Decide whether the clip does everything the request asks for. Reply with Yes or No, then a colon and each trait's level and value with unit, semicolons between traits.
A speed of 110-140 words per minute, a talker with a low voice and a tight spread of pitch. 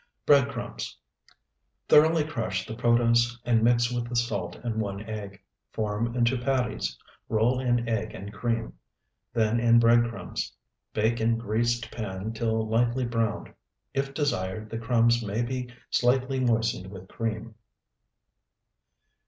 Yes: slow, 135 wpm; low, 115 Hz; narrow, 1.7 semitones